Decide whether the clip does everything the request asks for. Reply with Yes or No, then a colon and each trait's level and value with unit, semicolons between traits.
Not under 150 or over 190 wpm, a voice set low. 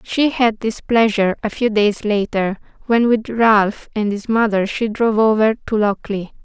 No: average, 175 wpm; high, 215 Hz